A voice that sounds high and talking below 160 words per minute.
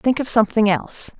No: high, 225 Hz; average, 200 wpm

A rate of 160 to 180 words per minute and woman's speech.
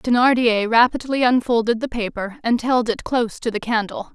Yes: average, 175 wpm; female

